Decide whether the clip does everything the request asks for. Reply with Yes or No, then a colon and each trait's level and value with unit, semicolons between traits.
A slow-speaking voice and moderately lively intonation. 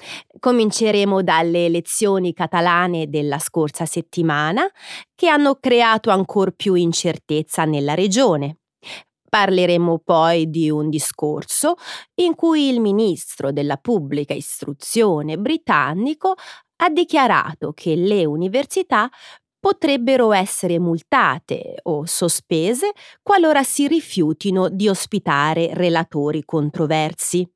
No: slow, 100 wpm; wide, 7.5 semitones